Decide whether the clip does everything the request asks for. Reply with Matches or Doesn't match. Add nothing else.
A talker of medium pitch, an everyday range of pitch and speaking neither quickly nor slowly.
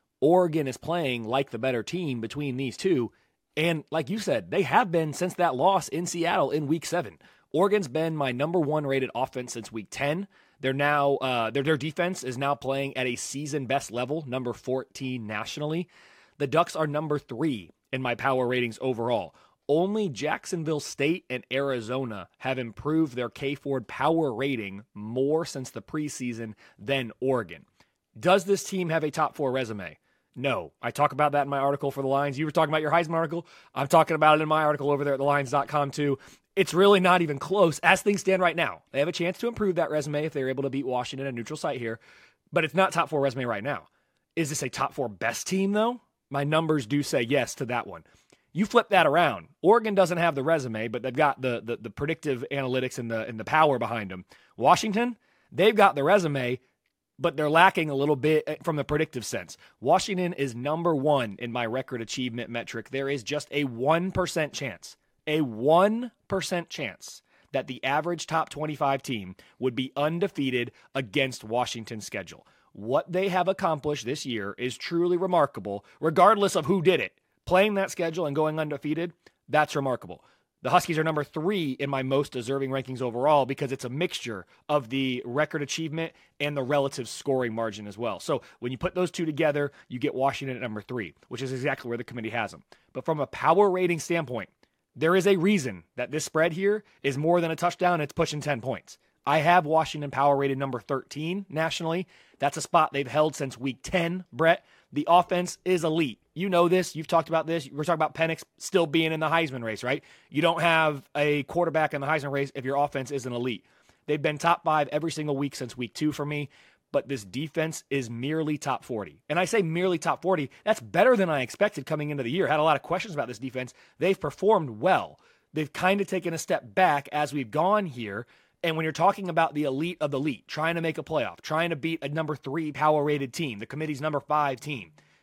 Doesn't match